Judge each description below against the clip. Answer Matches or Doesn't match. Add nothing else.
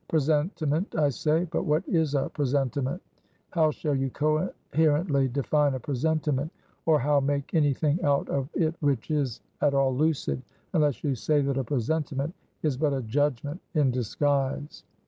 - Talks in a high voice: Doesn't match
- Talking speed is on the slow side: Doesn't match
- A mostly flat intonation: Matches